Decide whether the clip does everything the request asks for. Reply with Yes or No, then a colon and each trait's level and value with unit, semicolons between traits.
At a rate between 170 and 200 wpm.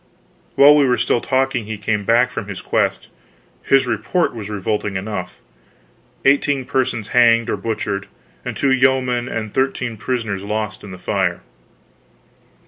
No: average, 145 wpm